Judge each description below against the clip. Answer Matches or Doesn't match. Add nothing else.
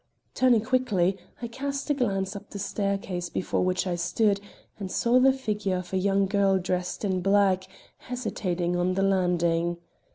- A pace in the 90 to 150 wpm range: Doesn't match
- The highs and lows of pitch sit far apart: Doesn't match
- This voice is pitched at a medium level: Doesn't match